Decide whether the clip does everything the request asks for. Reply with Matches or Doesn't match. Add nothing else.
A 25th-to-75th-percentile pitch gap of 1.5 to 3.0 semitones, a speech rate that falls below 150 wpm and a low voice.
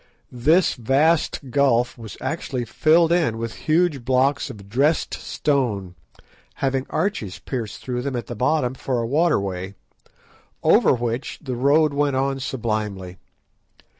Doesn't match